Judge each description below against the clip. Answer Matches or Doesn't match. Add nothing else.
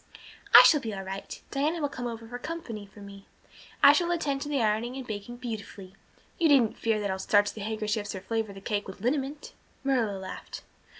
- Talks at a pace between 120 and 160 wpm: Doesn't match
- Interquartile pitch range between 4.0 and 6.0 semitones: Matches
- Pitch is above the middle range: Matches